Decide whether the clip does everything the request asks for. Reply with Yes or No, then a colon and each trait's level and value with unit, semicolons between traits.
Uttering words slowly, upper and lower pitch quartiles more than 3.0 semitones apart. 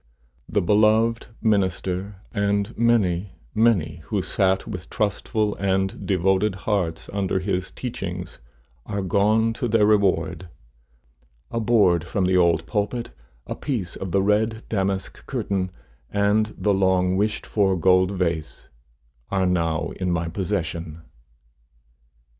No: slow, 125 wpm; narrow, 2.6 semitones